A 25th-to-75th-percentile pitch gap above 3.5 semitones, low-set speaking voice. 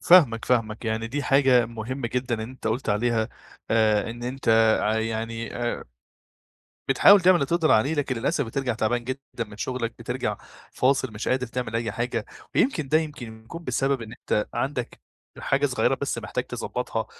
No: average, 3.2 semitones; low, 120 Hz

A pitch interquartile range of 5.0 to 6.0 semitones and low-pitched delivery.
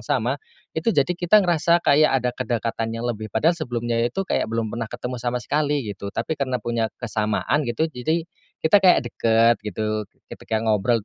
Yes: average, 5.3 semitones; low, 120 Hz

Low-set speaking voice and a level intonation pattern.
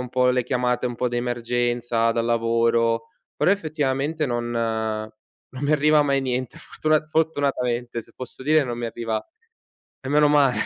No: low, 125 Hz; average, 3.4 semitones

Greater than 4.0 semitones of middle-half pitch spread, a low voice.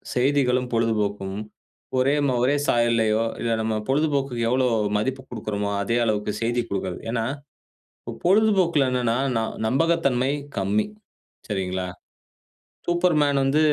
Yes: average, 4.5 semitones; low, 120 Hz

